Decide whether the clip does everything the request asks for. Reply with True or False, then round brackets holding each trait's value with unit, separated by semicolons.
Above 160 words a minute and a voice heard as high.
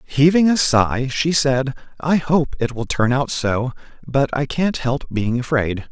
False (185 wpm; 135 Hz)